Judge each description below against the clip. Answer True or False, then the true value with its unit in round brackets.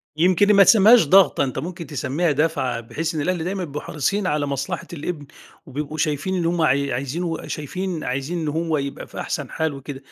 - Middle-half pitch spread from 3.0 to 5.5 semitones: True (3.9 semitones)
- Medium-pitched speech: True (155 Hz)